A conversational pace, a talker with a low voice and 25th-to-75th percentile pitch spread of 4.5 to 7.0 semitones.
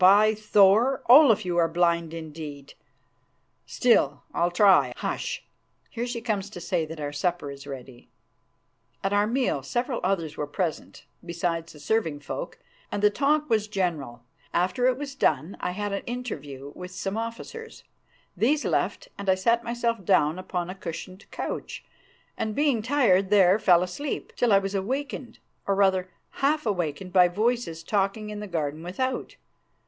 No: average, 160 wpm; high, 195 Hz; wide, 5.5 semitones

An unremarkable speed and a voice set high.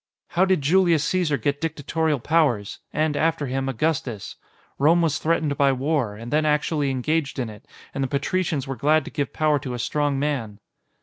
No: average, 185 wpm; medium, 145 Hz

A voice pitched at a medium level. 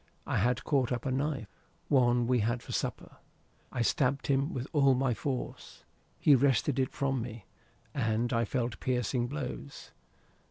No: low, 125 Hz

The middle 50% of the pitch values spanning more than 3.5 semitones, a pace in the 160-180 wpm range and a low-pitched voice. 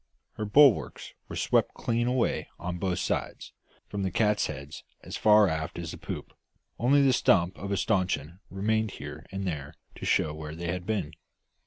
Yes: average, 4.4 semitones; average, 175 wpm; very low, 95 Hz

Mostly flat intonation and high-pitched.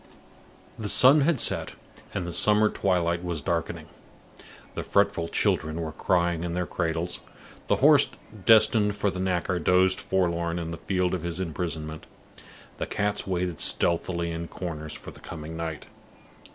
No: narrow, 2.3 semitones; very low, 85 Hz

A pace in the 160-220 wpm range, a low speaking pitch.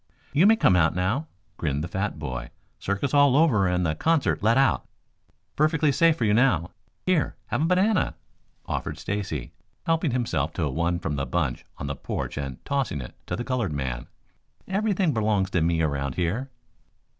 Yes: average, 180 wpm; low, 105 Hz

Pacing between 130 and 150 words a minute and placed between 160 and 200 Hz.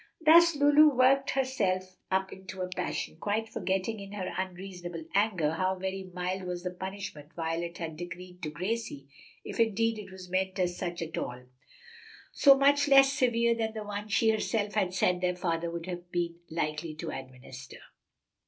No: average, 170 wpm; medium, 185 Hz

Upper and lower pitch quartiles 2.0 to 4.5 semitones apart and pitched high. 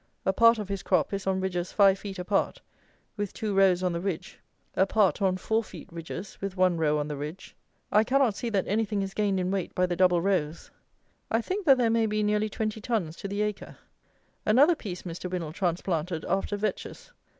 Yes: average, 2.9 semitones; high, 195 Hz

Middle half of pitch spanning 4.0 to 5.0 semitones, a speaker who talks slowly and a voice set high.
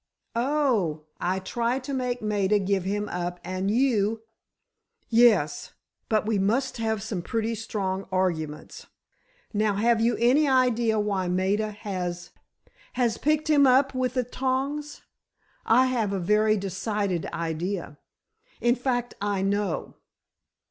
Yes: average, 4.3 semitones; slow, 125 wpm; high, 215 Hz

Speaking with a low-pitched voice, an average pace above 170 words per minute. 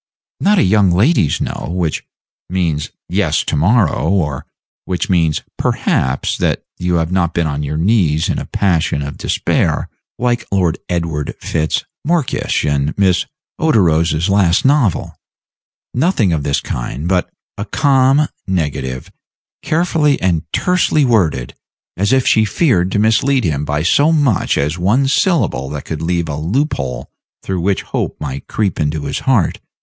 No: very low, 90 Hz; average, 155 wpm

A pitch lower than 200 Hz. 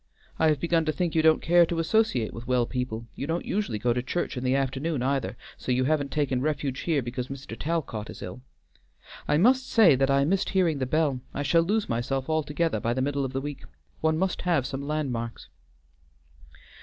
Yes: medium, 140 Hz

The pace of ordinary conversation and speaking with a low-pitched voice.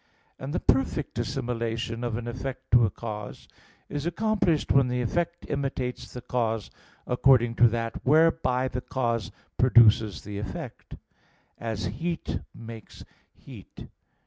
No: slow, 130 wpm; low, 125 Hz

